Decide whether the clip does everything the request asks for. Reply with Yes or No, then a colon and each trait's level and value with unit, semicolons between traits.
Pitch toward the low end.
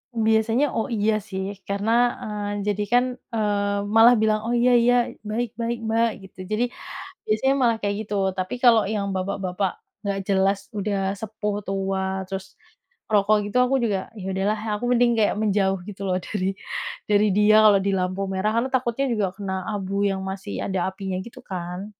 No: high, 205 Hz